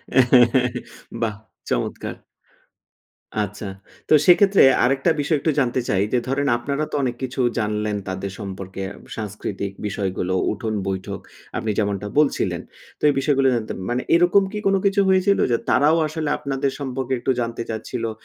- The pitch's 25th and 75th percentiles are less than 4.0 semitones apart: No, average, 5.3 semitones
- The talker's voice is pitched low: Yes, low, 125 Hz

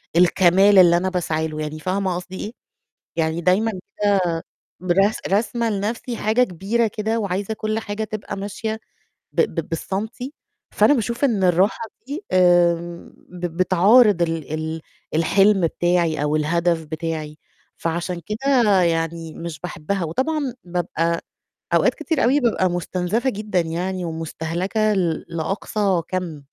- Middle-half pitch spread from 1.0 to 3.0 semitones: No, average, 4.2 semitones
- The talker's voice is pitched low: No, medium, 185 Hz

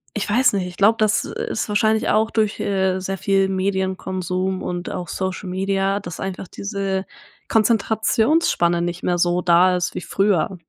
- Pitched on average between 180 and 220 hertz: Yes, high, 190 Hz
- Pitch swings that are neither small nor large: No, narrow, 2.1 semitones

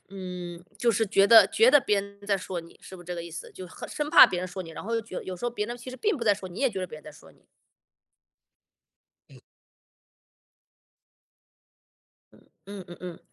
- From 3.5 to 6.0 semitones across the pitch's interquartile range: Yes, average, 4.1 semitones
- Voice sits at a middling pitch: No, high, 195 Hz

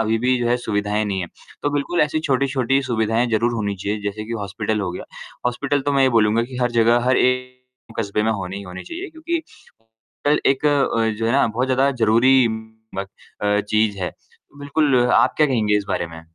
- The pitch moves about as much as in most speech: Yes, average, 4.1 semitones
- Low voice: Yes, low, 115 Hz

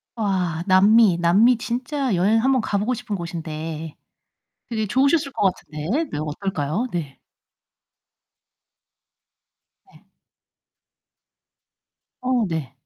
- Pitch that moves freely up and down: Yes, wide, 6.7 semitones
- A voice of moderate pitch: No, high, 200 Hz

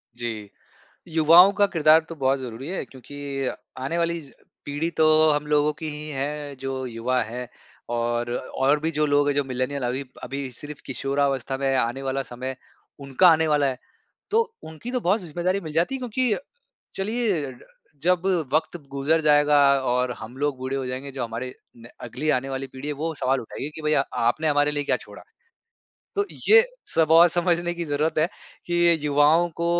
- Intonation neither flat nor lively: Yes, average, 3.7 semitones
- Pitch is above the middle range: No, medium, 145 Hz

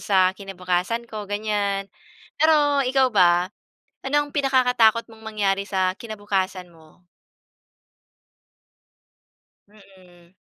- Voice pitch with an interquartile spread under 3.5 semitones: No, average, 4.0 semitones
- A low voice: No, high, 205 Hz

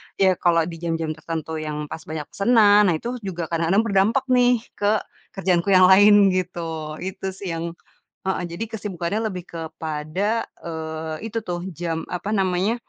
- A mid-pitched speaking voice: Yes, medium, 180 Hz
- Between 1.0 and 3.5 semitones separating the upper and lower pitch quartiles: No, average, 3.9 semitones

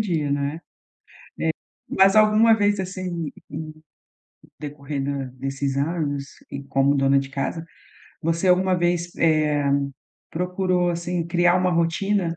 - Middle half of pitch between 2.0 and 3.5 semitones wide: No, average, 4.2 semitones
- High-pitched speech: No, medium, 165 Hz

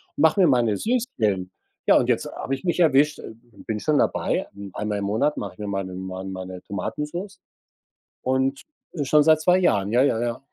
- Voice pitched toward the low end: Yes, low, 130 Hz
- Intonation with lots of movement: Yes, wide, 7.3 semitones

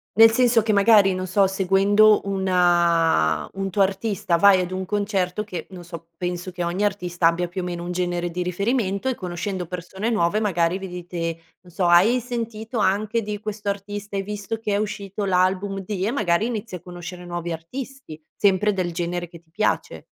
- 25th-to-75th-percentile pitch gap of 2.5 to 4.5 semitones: Yes, average, 2.9 semitones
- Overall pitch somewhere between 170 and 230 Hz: Yes, high, 190 Hz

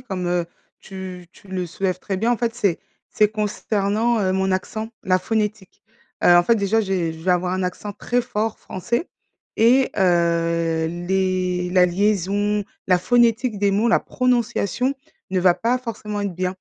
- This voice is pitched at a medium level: No, high, 195 Hz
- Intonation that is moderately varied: Yes, average, 3.4 semitones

